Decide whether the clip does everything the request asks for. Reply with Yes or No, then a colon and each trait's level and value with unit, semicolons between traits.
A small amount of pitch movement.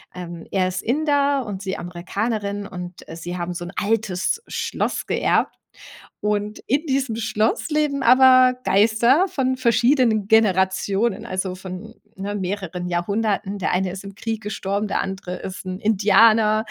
No: average, 3.7 semitones